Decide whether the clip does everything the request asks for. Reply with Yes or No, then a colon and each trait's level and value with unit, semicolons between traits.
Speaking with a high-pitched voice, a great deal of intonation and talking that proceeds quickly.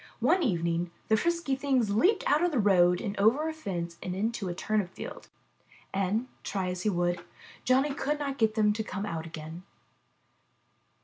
No: high, 210 Hz; wide, 7.1 semitones; average, 180 wpm